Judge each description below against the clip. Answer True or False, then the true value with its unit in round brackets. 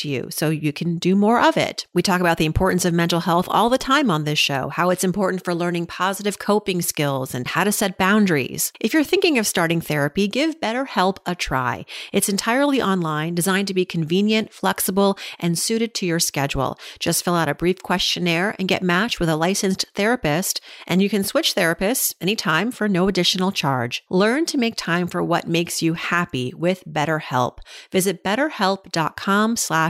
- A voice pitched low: False (185 Hz)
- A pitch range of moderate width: True (3.6 semitones)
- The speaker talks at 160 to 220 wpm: True (190 wpm)